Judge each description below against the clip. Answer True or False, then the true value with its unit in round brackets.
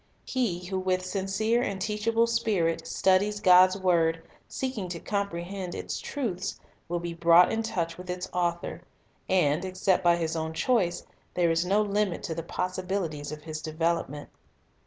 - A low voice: False (180 Hz)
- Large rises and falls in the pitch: False (3.0 semitones)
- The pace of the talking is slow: False (160 wpm)